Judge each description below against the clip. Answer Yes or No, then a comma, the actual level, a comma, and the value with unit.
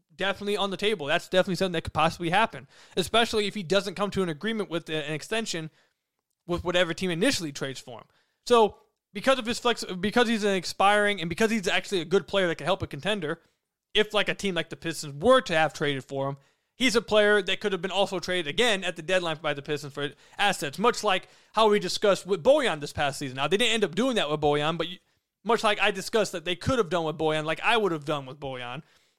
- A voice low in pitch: No, medium, 185 Hz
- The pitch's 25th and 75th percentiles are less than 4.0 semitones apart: No, average, 4.7 semitones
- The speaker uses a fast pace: Yes, fast, 245 wpm